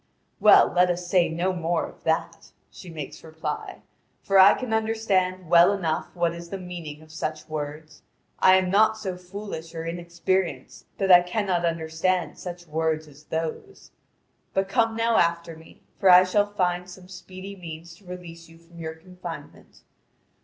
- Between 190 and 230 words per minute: No, average, 165 wpm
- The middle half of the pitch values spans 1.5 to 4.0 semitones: Yes, narrow, 2.6 semitones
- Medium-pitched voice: Yes, medium, 175 Hz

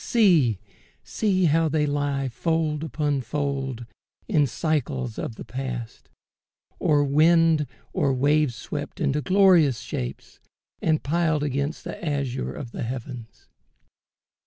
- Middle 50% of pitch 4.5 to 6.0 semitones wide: No, average, 3.5 semitones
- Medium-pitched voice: Yes, medium, 145 Hz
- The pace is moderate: No, slow, 115 wpm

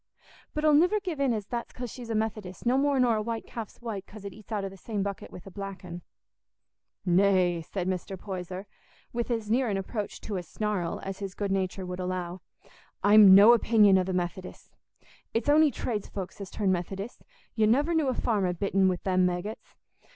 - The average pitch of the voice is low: No, high, 200 Hz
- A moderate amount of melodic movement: Yes, average, 3.6 semitones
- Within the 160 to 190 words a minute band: No, fast, 205 wpm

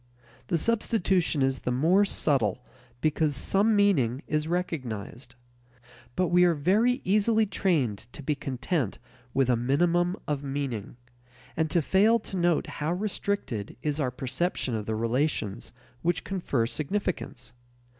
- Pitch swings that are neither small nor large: No, wide, 6.4 semitones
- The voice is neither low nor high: Yes, medium, 155 Hz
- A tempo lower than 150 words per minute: Yes, slow, 135 wpm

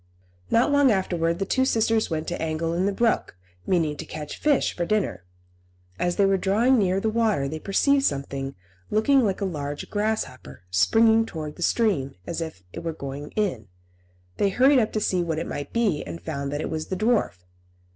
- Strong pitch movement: Yes, wide, 6.6 semitones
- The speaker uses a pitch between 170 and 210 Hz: Yes, medium, 185 Hz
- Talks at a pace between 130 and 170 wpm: No, average, 195 wpm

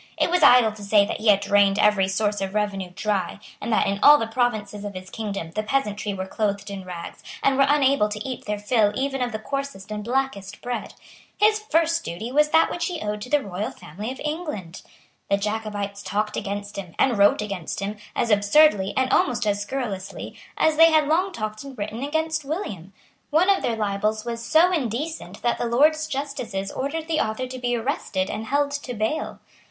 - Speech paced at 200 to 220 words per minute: Yes, fast, 205 wpm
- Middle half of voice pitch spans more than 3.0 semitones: Yes, wide, 5.5 semitones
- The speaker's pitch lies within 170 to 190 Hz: No, high, 220 Hz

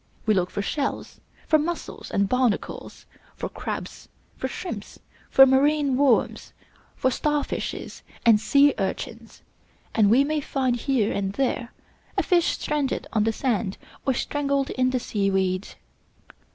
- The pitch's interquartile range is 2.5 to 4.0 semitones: No, average, 4.8 semitones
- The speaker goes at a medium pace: Yes, average, 145 wpm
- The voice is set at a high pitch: Yes, very high, 260 Hz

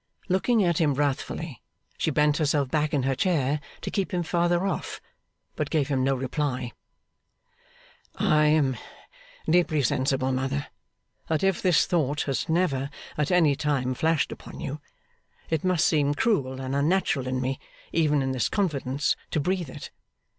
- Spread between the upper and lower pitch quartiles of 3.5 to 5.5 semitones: Yes, average, 3.8 semitones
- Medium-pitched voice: Yes, medium, 150 Hz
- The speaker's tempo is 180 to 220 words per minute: No, average, 155 wpm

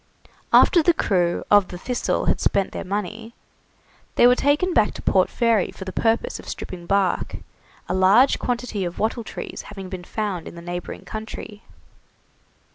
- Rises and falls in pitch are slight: No, average, 4.0 semitones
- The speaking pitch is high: Yes, high, 205 Hz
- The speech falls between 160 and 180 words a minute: Yes, average, 170 wpm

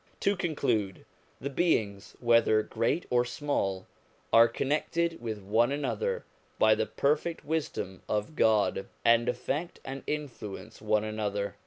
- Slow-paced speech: Yes, slow, 130 wpm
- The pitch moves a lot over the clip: Yes, wide, 5.7 semitones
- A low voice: Yes, low, 120 Hz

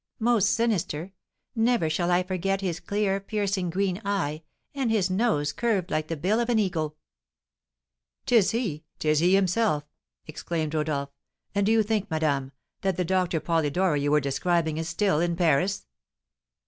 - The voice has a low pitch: No, medium, 180 Hz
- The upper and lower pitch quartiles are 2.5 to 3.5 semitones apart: No, average, 4.5 semitones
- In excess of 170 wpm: No, average, 160 wpm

